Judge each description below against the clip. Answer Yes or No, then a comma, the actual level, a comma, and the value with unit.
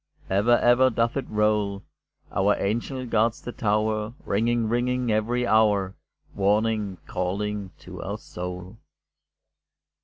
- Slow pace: Yes, slow, 115 wpm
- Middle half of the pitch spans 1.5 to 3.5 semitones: Yes, average, 2.7 semitones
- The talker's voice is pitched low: Yes, low, 110 Hz